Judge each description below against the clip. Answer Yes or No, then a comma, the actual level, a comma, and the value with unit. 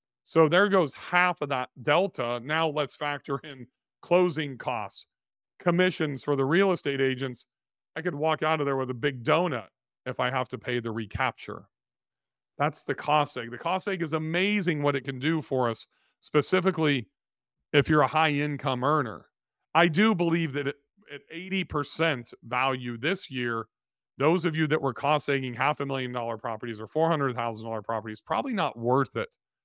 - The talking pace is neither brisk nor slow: Yes, average, 180 wpm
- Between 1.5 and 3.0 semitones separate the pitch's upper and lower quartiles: No, average, 4.2 semitones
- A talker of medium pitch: Yes, medium, 145 Hz